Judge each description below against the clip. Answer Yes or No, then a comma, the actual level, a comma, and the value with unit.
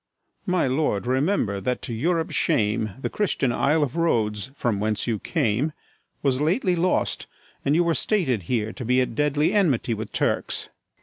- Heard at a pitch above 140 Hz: No, low, 130 Hz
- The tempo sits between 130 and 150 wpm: No, average, 170 wpm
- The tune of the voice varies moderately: No, wide, 6.5 semitones